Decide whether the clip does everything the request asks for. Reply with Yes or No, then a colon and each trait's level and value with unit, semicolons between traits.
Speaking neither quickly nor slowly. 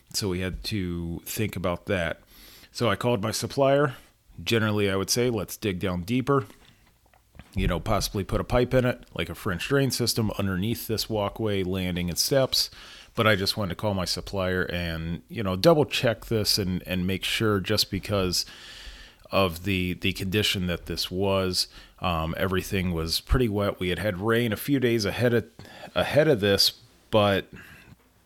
Yes: average, 180 wpm